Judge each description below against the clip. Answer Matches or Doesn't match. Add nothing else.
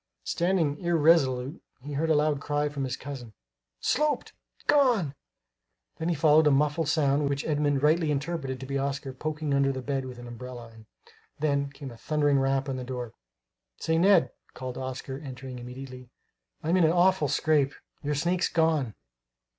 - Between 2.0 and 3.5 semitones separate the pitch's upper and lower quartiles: Matches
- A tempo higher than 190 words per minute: Doesn't match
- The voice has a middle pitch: Matches